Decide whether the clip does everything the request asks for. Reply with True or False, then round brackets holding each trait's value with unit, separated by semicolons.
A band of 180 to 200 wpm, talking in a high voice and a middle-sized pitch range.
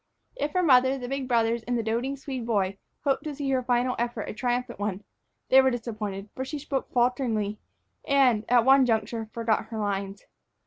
True (190 wpm; 240 Hz; 3.2 semitones)